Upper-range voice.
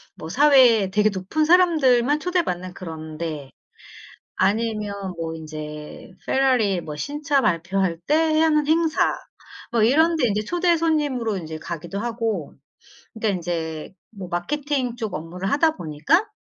Yes: high, 215 Hz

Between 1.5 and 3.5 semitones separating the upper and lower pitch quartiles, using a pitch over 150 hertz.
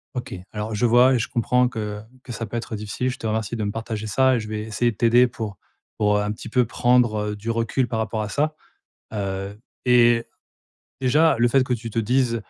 No: narrow, 2.5 semitones; low, 115 Hz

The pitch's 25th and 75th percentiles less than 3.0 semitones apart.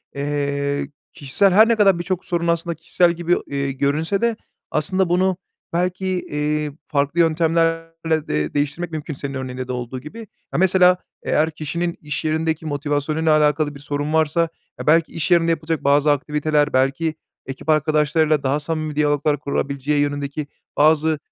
Yes: narrow, 2.6 semitones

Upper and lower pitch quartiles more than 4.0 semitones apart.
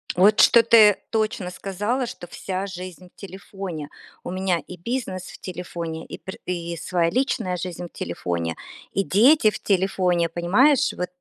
No: average, 3.0 semitones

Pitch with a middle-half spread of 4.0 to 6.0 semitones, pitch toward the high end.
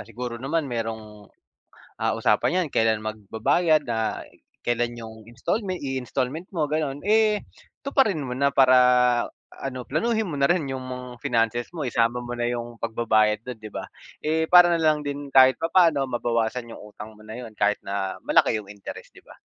No: average, 5.0 semitones; low, 125 Hz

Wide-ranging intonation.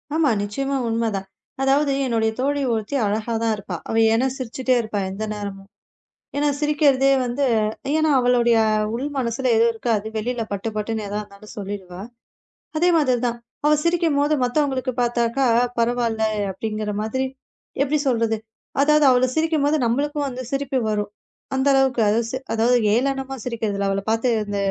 No: average, 3.8 semitones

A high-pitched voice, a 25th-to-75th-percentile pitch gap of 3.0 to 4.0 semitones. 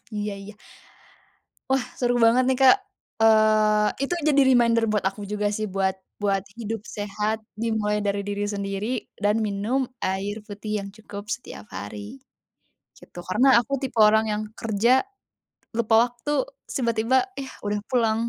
No: high, 215 Hz; narrow, 2.5 semitones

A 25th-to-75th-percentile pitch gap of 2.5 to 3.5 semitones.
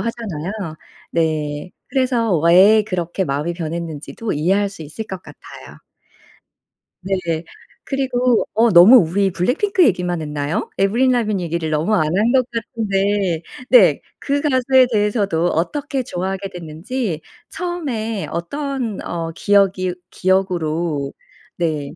No: wide, 5.6 semitones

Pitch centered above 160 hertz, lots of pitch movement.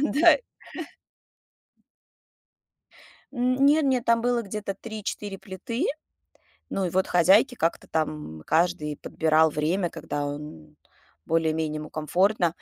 Yes: medium, 185 Hz; wide, 6.7 semitones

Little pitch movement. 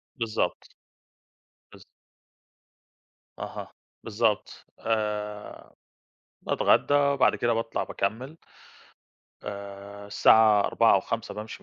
Yes: narrow, 2.0 semitones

